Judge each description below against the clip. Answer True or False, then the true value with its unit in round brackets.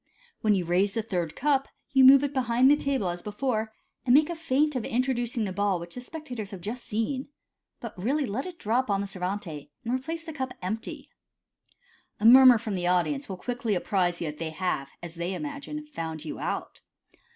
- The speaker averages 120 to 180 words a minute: False (205 wpm)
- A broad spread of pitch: True (6.3 semitones)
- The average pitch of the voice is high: True (225 Hz)